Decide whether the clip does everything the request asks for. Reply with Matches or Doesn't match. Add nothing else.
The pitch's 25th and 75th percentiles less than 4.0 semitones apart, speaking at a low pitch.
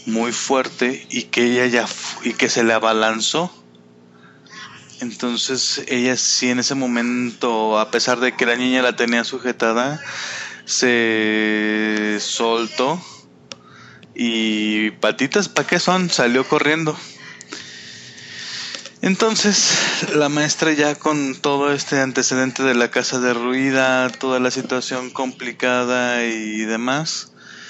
Matches